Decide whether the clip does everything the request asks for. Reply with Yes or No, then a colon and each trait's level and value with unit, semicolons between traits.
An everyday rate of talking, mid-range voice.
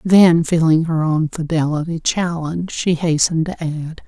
Yes: average, 145 wpm; medium, 165 Hz